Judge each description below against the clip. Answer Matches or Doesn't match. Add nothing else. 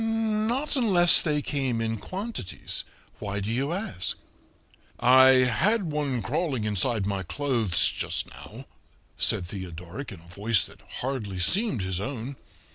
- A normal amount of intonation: Doesn't match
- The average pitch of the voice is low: Matches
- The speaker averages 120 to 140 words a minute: Matches